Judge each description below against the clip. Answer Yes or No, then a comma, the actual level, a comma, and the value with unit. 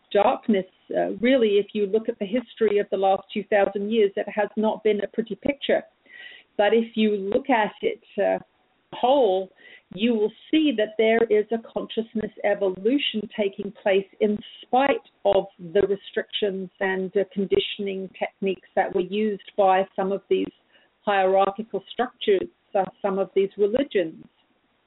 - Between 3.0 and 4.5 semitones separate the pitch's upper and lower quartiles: No, narrow, 2.5 semitones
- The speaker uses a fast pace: No, average, 150 wpm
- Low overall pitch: No, high, 210 Hz